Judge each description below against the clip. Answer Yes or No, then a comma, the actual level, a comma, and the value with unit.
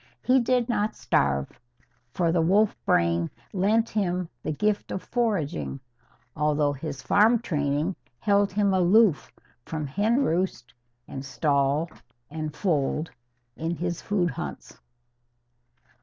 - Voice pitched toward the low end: No, medium, 170 Hz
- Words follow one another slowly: Yes, slow, 120 wpm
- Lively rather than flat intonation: Yes, wide, 6.1 semitones